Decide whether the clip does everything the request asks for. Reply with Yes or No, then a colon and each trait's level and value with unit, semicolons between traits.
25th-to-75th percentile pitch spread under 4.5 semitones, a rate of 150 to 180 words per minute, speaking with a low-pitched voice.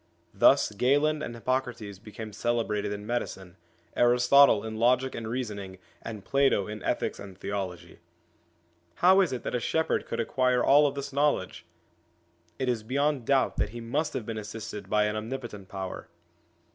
Yes: average, 4.1 semitones; average, 160 wpm; low, 115 Hz